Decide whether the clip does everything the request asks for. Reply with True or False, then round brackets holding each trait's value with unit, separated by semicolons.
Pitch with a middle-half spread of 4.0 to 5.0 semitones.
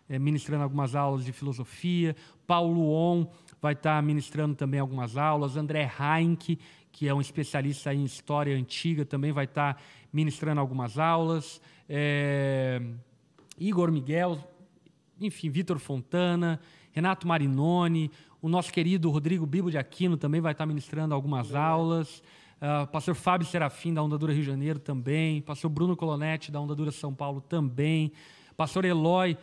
False (2.6 semitones)